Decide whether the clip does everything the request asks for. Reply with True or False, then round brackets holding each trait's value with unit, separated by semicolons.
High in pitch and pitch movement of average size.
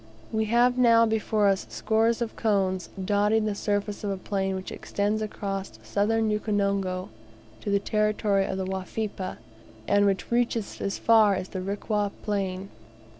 False (205 Hz; 2.0 semitones)